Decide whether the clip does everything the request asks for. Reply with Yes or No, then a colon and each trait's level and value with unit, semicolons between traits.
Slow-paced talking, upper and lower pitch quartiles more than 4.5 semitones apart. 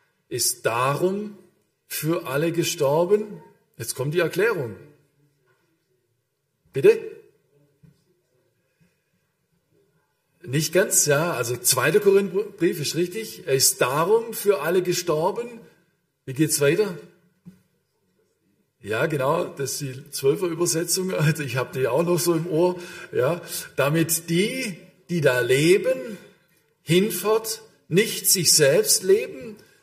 Yes: slow, 110 wpm; wide, 5.4 semitones